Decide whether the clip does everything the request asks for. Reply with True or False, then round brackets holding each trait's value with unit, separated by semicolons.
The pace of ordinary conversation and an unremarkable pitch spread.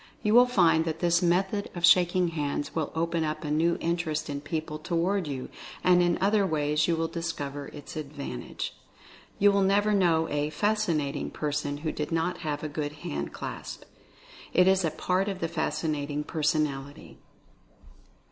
True (165 wpm; 3.1 semitones)